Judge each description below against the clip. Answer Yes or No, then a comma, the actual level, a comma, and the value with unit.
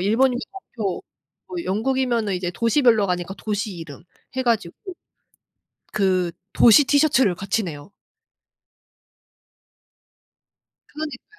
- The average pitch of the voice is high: Yes, high, 215 Hz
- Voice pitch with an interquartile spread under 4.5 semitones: No, wide, 5.6 semitones